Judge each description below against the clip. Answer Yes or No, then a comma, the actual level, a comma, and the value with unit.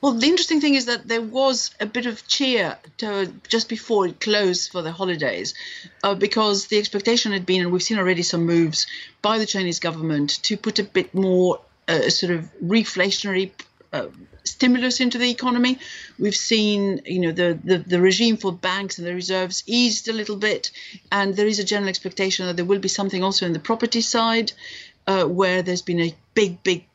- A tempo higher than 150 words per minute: Yes, average, 200 wpm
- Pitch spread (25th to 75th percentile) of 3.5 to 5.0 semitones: Yes, average, 3.8 semitones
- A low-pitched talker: No, high, 200 Hz